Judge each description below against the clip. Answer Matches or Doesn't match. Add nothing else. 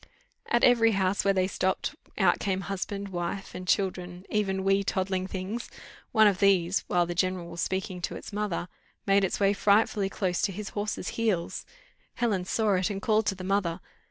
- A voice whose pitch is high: Matches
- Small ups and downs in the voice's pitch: Matches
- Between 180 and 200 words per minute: Matches